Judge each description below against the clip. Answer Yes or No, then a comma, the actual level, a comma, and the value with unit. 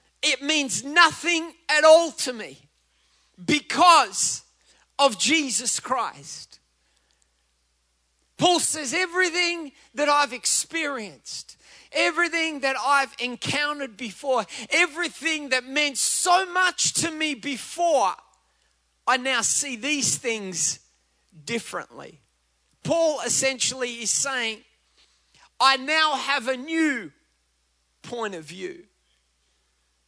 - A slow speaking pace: Yes, slow, 95 wpm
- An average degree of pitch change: No, wide, 8.1 semitones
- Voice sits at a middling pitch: No, very high, 270 Hz